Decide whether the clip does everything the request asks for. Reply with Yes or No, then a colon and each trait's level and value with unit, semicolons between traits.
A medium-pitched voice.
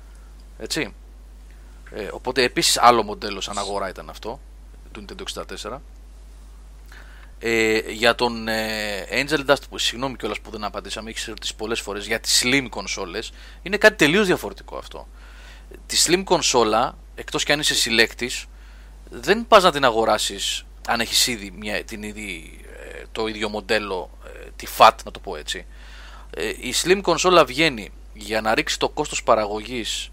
No: low, 110 Hz